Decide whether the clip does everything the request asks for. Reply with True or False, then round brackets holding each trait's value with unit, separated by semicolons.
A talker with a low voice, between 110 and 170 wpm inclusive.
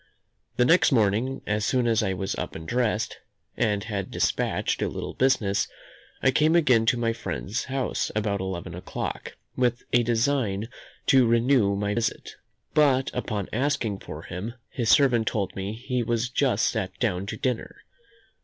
True (115 Hz; 165 wpm)